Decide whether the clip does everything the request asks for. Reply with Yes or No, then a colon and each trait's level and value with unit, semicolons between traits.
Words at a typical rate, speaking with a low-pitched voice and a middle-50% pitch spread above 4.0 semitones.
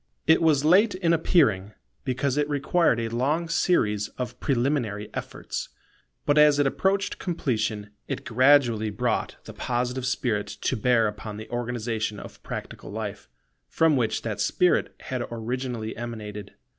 Yes: average, 145 wpm; low, 125 Hz; average, 5.0 semitones